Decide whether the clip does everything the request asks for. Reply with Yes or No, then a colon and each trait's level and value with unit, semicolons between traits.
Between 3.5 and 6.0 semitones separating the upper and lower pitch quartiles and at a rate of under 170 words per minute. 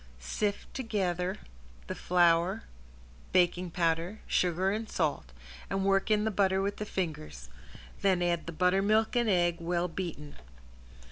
No: average, 2.8 semitones; slow, 135 wpm